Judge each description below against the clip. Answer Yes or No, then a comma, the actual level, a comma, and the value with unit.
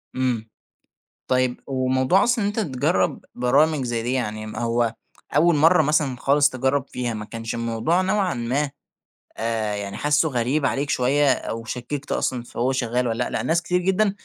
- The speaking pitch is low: Yes, low, 130 Hz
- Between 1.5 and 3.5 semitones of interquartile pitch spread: No, average, 4.1 semitones